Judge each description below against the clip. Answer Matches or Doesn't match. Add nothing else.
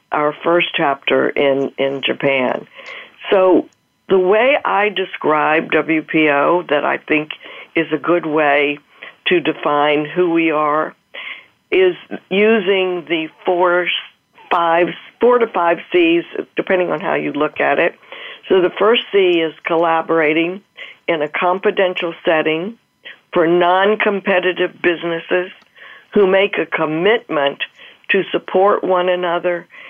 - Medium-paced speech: Doesn't match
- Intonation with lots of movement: Doesn't match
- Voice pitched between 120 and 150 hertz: Doesn't match